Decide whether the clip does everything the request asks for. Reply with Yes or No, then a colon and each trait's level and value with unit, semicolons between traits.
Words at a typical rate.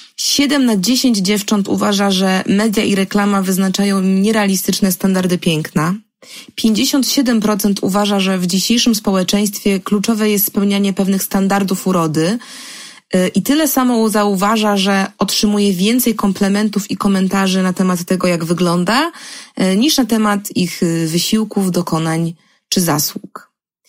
Yes: average, 120 wpm